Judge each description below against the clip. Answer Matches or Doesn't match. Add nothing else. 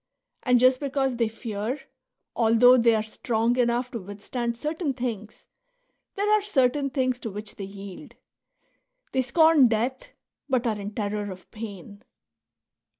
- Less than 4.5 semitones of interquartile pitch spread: Matches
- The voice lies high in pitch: Matches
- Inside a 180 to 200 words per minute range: Doesn't match